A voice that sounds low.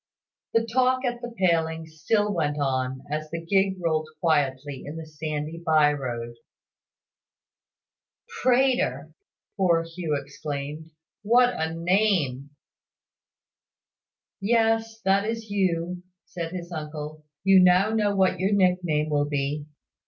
No: medium, 165 Hz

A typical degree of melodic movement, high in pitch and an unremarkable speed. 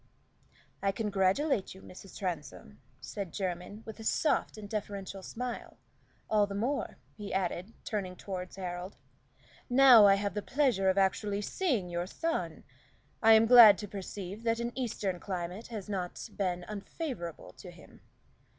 Yes: average, 3.3 semitones; high, 200 Hz; average, 150 wpm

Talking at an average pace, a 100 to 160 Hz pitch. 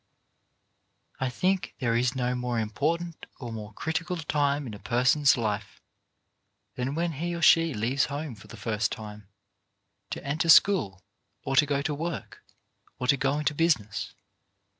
Yes: average, 160 wpm; low, 135 Hz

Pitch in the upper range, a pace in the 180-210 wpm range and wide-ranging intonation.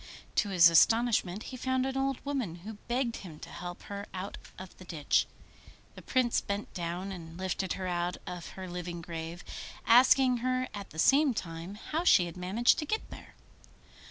Yes: high, 195 Hz; average, 185 wpm; wide, 5.9 semitones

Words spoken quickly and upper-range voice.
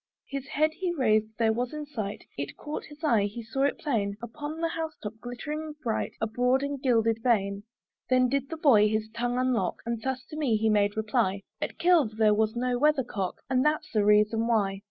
Yes: fast, 215 wpm; high, 240 Hz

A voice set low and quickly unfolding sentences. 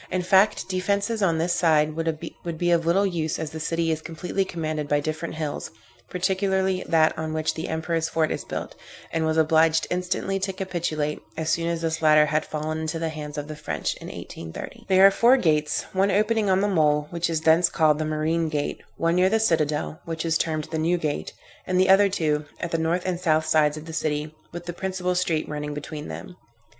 No: medium, 165 Hz; fast, 215 wpm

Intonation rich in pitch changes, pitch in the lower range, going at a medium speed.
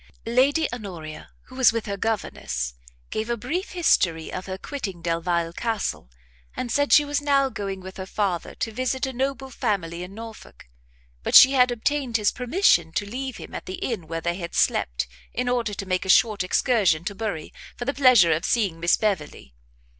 No: wide, 6.4 semitones; high, 215 Hz; average, 190 wpm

